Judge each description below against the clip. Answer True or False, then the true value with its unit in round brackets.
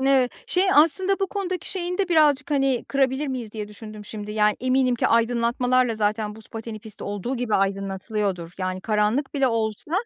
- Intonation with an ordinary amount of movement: True (4.6 semitones)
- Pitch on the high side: True (235 Hz)